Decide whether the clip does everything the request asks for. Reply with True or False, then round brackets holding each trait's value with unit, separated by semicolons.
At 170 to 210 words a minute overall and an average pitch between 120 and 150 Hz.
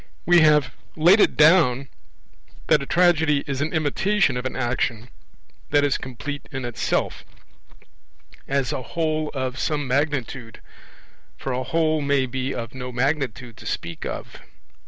False (145 wpm; 140 Hz)